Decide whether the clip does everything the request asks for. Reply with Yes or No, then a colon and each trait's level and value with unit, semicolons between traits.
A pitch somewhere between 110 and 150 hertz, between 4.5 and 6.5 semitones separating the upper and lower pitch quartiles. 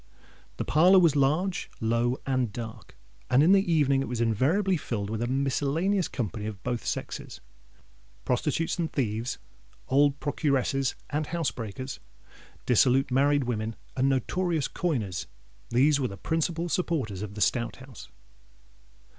Yes: low, 135 Hz; average, 5.2 semitones